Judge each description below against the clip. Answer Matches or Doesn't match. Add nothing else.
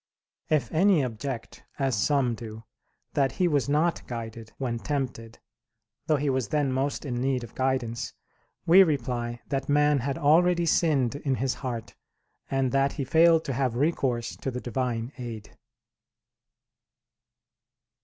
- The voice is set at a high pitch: Doesn't match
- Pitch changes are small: Doesn't match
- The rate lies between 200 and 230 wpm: Doesn't match